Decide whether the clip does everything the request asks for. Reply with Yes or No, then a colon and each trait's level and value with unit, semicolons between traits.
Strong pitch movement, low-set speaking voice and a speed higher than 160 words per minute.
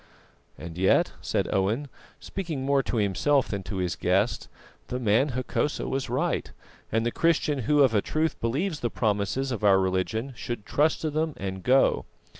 Yes: wide, 6.1 semitones; low, 125 Hz; average, 175 wpm